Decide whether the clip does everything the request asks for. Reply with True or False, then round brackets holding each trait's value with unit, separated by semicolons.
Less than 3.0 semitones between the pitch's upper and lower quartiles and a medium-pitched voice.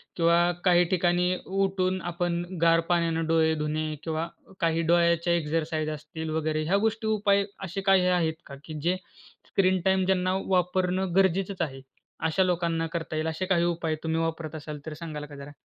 True (2.5 semitones; 170 Hz)